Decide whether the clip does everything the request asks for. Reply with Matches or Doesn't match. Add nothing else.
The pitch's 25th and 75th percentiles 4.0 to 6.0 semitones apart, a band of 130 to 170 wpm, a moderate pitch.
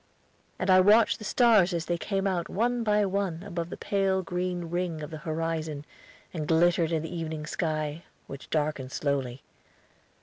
Doesn't match